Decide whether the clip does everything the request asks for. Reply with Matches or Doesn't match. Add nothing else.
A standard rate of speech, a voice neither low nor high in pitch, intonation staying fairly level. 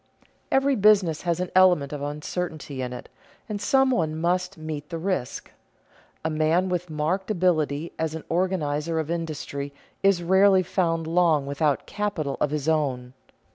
Doesn't match